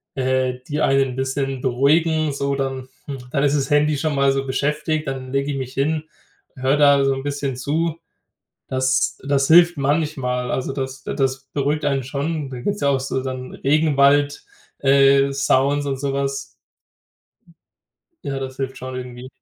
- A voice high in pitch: No, medium, 140 Hz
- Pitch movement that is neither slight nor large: No, narrow, 1.6 semitones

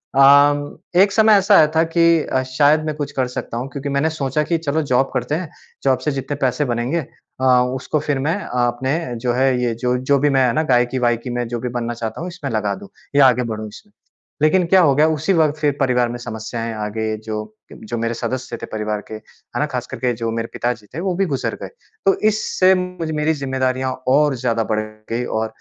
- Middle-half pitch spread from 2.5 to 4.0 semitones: No, average, 4.4 semitones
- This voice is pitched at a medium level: No, low, 130 Hz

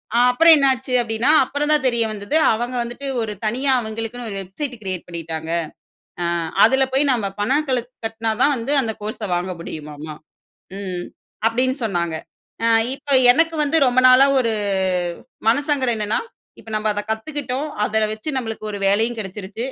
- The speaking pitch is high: Yes, high, 230 Hz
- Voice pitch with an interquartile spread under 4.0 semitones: No, average, 4.3 semitones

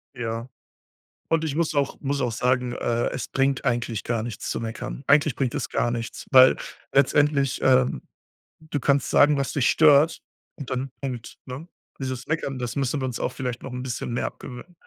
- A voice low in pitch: Yes, low, 130 Hz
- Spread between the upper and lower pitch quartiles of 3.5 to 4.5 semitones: No, narrow, 2.6 semitones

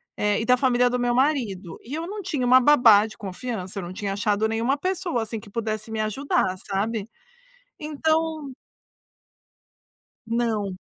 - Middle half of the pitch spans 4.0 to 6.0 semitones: Yes, average, 4.9 semitones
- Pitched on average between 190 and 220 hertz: No, high, 230 Hz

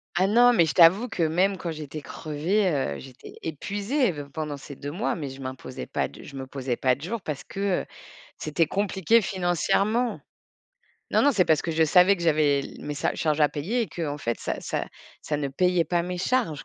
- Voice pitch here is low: No, medium, 165 Hz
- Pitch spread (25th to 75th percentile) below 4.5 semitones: No, average, 5.1 semitones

